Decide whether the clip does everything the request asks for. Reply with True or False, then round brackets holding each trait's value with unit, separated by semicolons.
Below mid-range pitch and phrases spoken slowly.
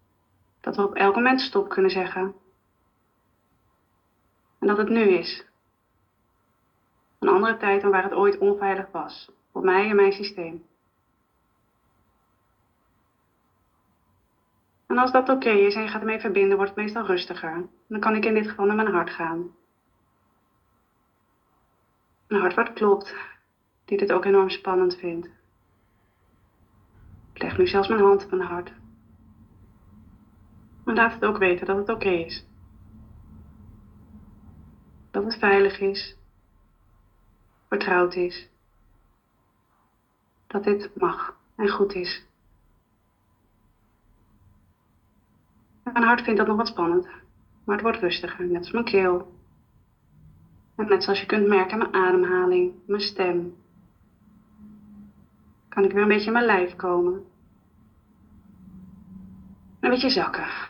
False (175 Hz; 130 wpm)